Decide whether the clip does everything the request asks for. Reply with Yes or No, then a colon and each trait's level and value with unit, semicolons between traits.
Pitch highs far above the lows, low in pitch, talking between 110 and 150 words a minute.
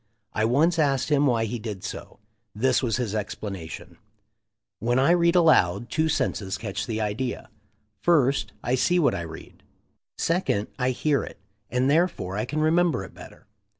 No: wide, 6.4 semitones; low, 125 Hz; average, 170 wpm